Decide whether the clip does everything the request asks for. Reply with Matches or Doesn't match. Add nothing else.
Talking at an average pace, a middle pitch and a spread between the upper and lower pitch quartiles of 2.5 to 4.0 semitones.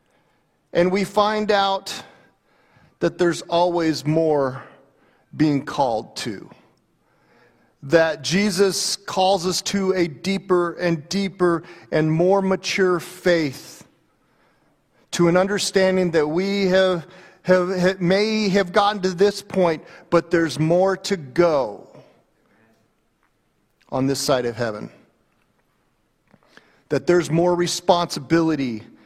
Doesn't match